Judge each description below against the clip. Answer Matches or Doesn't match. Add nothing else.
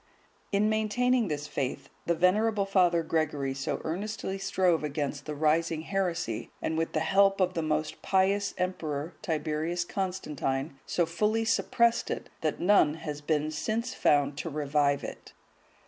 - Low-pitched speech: Doesn't match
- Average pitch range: Matches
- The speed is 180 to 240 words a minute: Doesn't match